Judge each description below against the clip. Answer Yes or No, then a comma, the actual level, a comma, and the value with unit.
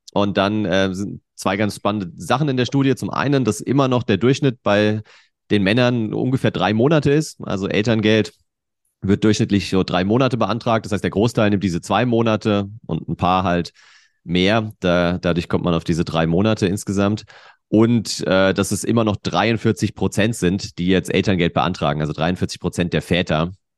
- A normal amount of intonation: Yes, average, 3.5 semitones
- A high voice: No, low, 105 Hz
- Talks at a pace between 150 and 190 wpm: Yes, average, 185 wpm